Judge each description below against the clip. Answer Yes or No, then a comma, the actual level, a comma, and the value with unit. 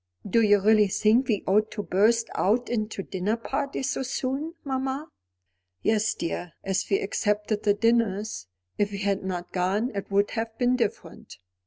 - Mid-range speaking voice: No, high, 215 Hz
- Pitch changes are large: No, average, 3.1 semitones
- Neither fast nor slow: Yes, average, 165 wpm